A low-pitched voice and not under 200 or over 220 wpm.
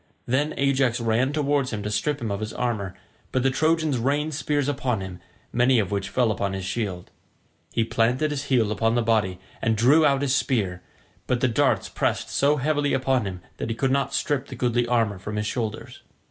Yes: low, 120 Hz; fast, 205 wpm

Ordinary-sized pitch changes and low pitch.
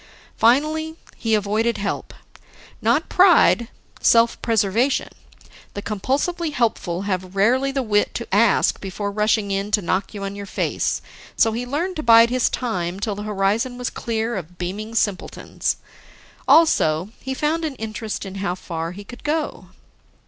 No: average, 4.0 semitones; high, 220 Hz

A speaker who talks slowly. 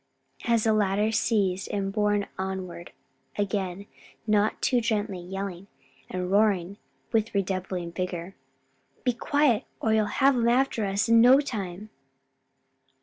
Yes: slow, 130 wpm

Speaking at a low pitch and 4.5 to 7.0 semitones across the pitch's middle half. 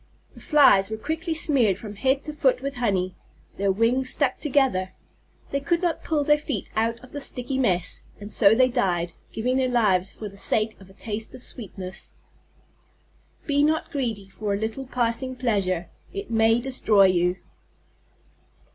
No: high, 230 Hz; average, 5.2 semitones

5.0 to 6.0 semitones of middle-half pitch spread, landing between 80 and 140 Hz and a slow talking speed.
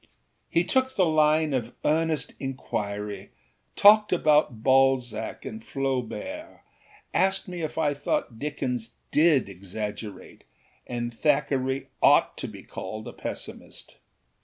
Yes: average, 5.3 semitones; low, 135 Hz; slow, 120 wpm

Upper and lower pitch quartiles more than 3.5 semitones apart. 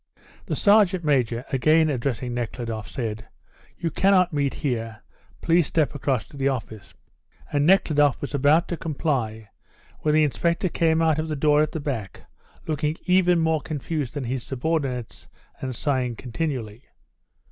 Yes: average, 4.5 semitones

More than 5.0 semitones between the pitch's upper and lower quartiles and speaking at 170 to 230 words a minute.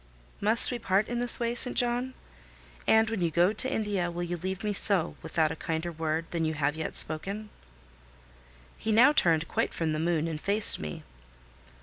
Yes: wide, 5.4 semitones; average, 195 wpm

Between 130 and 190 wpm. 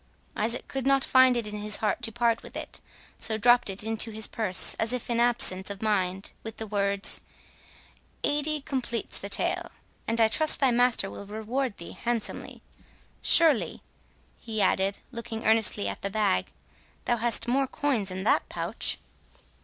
Yes: average, 160 wpm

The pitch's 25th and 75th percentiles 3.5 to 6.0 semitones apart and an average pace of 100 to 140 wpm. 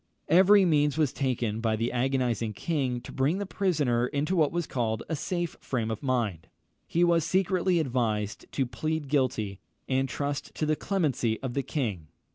No: average, 5.3 semitones; average, 175 wpm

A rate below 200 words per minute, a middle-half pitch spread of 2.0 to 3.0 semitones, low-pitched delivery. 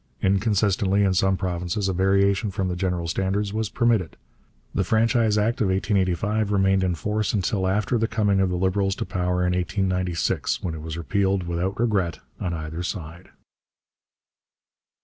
Yes: average, 160 wpm; narrow, 2.4 semitones; very low, 95 Hz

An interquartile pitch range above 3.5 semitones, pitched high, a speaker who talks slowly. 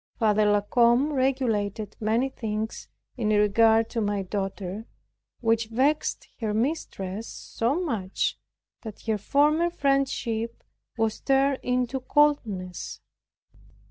Yes: average, 4.2 semitones; high, 225 Hz; slow, 110 wpm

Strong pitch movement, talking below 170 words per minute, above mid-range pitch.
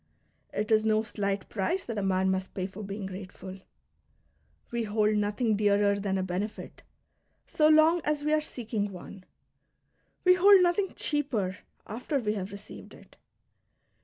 Yes: wide, 5.7 semitones; average, 160 wpm; high, 210 Hz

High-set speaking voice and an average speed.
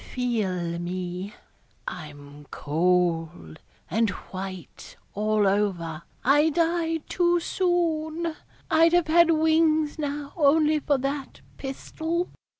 No: very high, 275 Hz; slow, 100 wpm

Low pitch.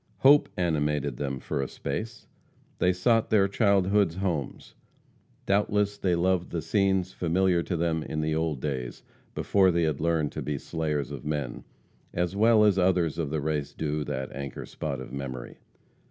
Yes: very low, 85 Hz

